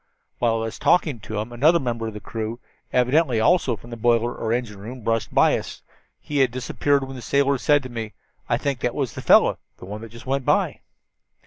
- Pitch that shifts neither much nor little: Yes, average, 3.1 semitones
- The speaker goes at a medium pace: No, fast, 225 wpm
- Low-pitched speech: Yes, low, 120 Hz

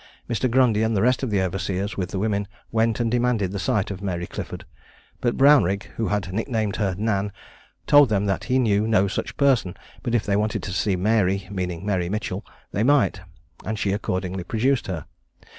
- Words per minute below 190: No, average, 195 wpm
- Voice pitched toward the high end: No, low, 105 Hz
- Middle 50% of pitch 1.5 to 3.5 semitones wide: Yes, average, 2.9 semitones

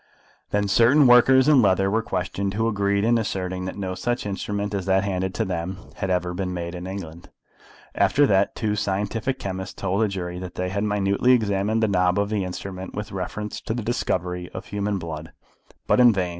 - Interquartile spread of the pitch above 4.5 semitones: No, narrow, 2.5 semitones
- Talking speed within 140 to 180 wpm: No, average, 200 wpm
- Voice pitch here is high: No, low, 100 Hz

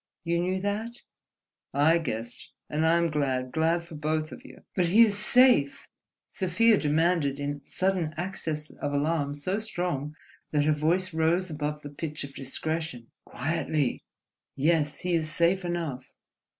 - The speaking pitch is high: No, medium, 160 Hz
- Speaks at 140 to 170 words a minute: Yes, average, 150 wpm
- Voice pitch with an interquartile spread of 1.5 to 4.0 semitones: Yes, average, 3.5 semitones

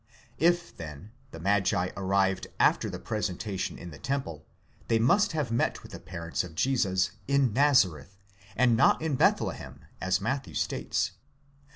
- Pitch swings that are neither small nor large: No, wide, 6.6 semitones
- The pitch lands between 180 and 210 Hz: No, low, 100 Hz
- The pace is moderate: Yes, average, 150 wpm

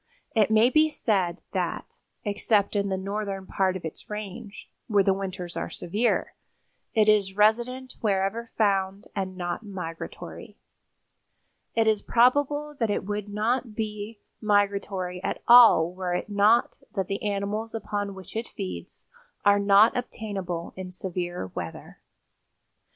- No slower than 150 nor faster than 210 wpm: No, average, 140 wpm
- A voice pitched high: Yes, high, 205 Hz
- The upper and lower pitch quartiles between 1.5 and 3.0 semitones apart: Yes, narrow, 2.6 semitones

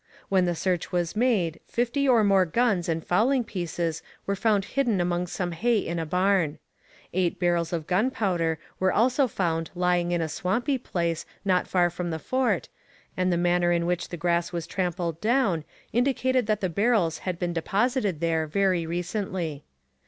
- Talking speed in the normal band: Yes, average, 175 wpm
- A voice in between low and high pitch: Yes, medium, 180 Hz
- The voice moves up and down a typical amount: Yes, average, 3.9 semitones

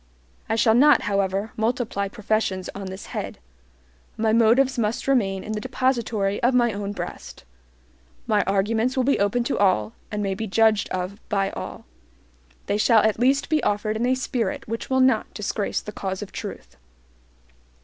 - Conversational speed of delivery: Yes, average, 170 wpm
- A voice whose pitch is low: No, high, 220 Hz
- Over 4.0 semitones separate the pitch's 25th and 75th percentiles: No, average, 3.5 semitones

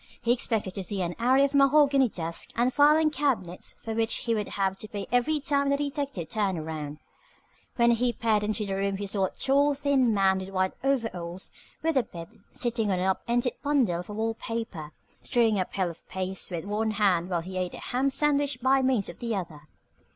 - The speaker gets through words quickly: Yes, fast, 210 wpm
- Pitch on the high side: Yes, high, 220 Hz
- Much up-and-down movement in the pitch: Yes, wide, 5.9 semitones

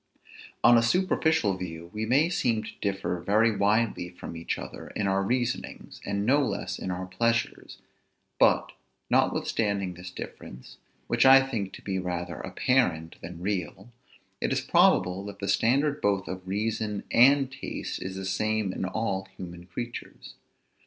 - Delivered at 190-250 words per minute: No, average, 155 wpm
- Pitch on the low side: Yes, low, 100 Hz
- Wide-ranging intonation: No, average, 4.0 semitones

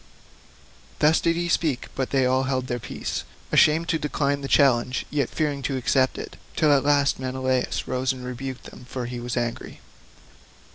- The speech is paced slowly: No, average, 180 wpm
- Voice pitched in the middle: No, low, 130 Hz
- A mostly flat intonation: Yes, narrow, 2.2 semitones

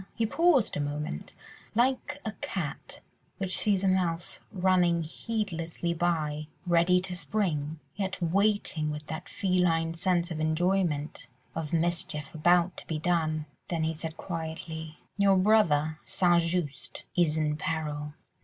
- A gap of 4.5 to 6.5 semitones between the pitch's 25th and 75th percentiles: No, average, 3.0 semitones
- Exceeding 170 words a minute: No, slow, 135 wpm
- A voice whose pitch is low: No, medium, 170 Hz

